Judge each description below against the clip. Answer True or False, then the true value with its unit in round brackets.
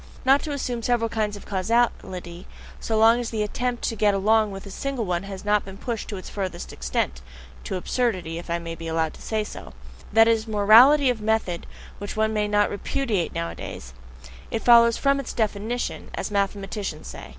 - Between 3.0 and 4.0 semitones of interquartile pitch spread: True (3.5 semitones)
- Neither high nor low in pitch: False (210 Hz)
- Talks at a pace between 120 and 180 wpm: False (195 wpm)